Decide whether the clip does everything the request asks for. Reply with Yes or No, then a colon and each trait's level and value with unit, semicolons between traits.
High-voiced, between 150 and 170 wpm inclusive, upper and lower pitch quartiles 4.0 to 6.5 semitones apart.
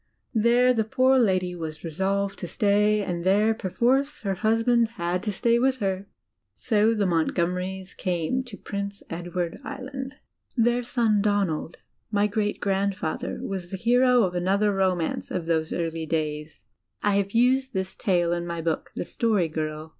Yes: high, 200 Hz; average, 160 wpm; average, 4.6 semitones